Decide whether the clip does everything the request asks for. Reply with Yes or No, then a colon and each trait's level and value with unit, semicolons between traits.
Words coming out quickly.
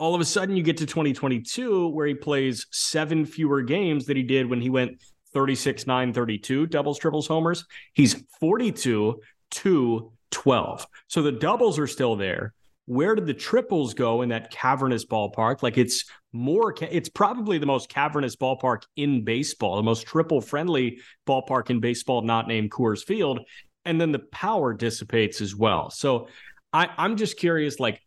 No: average, 170 wpm